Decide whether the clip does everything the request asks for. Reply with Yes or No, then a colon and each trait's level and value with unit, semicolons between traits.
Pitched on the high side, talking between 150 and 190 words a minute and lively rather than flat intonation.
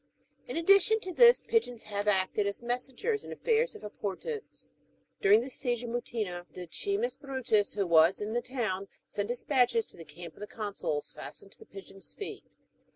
Yes: high, 230 Hz; average, 170 wpm; wide, 8.5 semitones